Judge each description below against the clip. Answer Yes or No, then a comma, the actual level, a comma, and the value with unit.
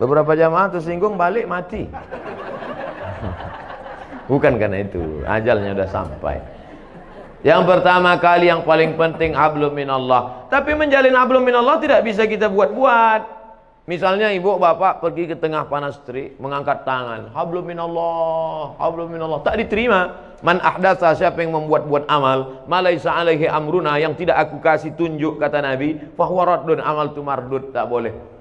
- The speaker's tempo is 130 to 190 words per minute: Yes, average, 135 wpm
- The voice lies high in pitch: No, medium, 160 Hz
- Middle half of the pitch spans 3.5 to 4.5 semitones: Yes, average, 3.8 semitones